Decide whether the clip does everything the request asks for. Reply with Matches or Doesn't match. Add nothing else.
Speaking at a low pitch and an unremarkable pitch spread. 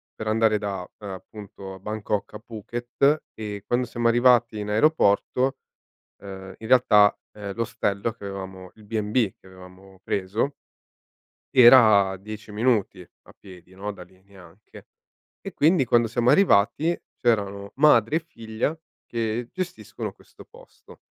Matches